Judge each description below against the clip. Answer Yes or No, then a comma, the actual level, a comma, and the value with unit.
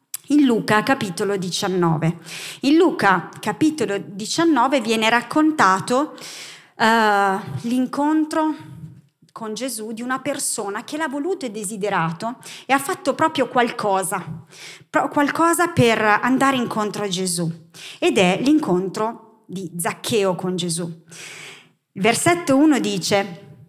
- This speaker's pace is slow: Yes, slow, 110 wpm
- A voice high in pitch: Yes, high, 215 Hz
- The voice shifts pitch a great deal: Yes, wide, 6.4 semitones